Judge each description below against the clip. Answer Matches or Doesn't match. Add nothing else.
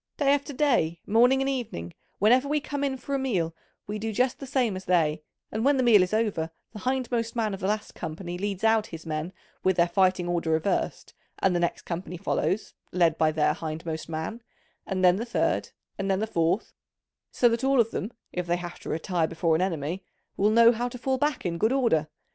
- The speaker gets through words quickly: Matches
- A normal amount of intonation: Doesn't match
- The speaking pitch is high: Matches